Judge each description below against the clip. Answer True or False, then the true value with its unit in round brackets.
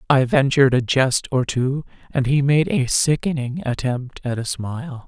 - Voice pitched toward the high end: False (135 Hz)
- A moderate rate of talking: True (175 wpm)